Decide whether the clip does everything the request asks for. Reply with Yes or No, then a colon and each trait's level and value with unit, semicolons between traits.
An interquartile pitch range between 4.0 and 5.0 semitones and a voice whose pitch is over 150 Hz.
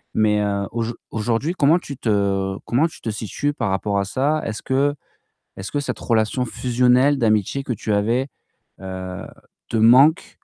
No: average, 4.7 semitones; low, 115 Hz